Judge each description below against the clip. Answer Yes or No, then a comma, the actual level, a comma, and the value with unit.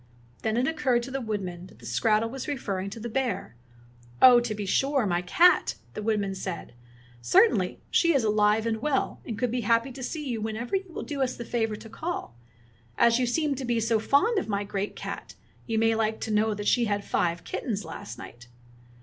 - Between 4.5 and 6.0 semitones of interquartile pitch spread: No, average, 3.8 semitones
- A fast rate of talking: Yes, fast, 220 wpm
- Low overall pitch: No, high, 225 Hz